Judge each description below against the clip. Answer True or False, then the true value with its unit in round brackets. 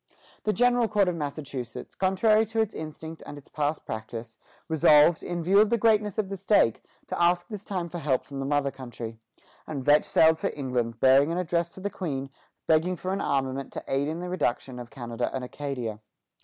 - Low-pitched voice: False (155 Hz)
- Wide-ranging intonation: True (5.7 semitones)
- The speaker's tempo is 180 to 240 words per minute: True (205 wpm)